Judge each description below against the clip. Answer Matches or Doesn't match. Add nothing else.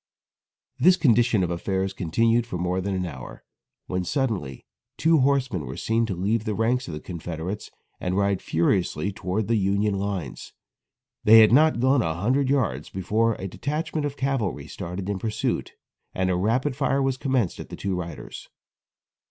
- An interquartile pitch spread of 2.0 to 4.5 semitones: Doesn't match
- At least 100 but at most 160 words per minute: Doesn't match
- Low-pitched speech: Matches